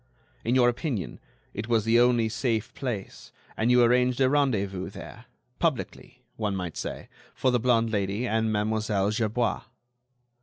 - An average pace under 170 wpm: Yes, average, 150 wpm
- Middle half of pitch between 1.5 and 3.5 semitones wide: Yes, average, 2.7 semitones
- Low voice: Yes, low, 115 Hz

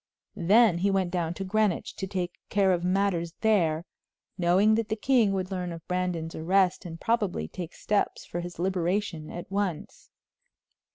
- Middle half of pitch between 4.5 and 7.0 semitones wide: No, average, 2.7 semitones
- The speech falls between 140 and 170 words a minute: Yes, average, 165 wpm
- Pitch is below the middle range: No, medium, 185 Hz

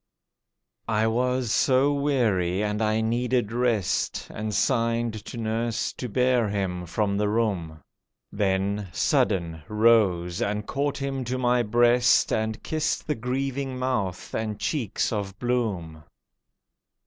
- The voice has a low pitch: Yes, low, 110 Hz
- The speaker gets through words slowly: Yes, slow, 125 wpm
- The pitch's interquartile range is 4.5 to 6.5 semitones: No, average, 3.7 semitones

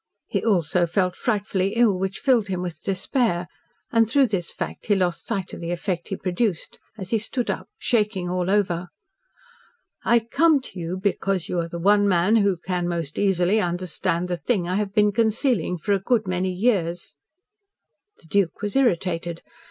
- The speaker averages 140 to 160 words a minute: No, average, 180 wpm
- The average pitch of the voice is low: No, high, 190 Hz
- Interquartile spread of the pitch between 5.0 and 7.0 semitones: No, average, 3.3 semitones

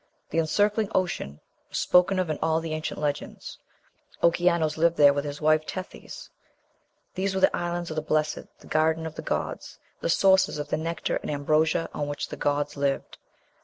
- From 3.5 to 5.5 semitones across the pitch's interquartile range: No, narrow, 2.6 semitones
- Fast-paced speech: No, average, 185 wpm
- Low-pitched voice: No, medium, 160 Hz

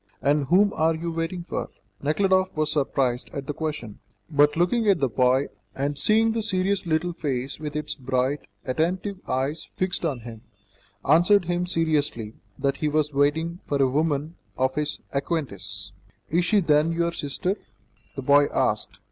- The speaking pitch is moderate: Yes, medium, 150 Hz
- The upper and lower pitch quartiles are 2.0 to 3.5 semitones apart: No, average, 4.0 semitones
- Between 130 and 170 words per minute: Yes, average, 165 wpm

